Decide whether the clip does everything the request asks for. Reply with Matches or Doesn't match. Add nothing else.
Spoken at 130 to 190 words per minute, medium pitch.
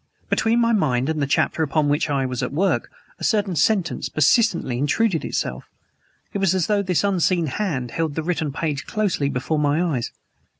Matches